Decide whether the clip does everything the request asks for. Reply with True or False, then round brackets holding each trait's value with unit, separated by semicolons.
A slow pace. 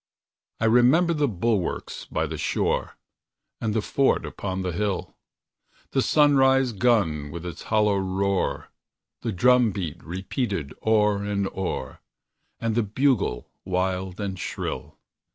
True (130 wpm)